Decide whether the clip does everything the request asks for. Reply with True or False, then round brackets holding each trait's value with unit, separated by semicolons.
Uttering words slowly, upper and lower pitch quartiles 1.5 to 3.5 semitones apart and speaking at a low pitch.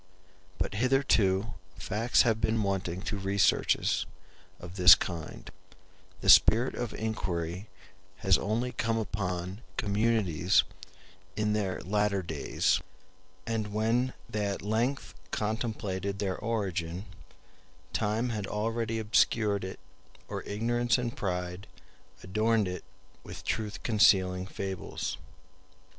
True (110 wpm; 3.1 semitones; 105 Hz)